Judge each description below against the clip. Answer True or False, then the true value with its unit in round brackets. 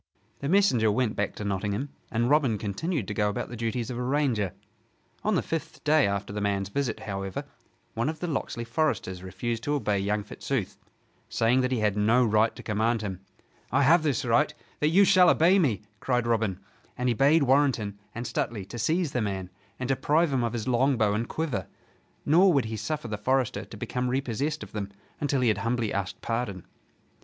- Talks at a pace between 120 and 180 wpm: False (200 wpm)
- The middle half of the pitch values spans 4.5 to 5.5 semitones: True (5.2 semitones)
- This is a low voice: True (120 Hz)